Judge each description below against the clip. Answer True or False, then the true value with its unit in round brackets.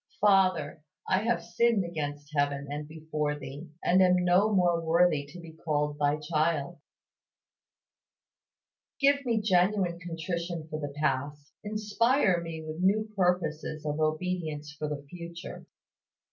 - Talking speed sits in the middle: False (130 wpm)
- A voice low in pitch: False (165 Hz)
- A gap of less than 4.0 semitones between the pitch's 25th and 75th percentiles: True (3.6 semitones)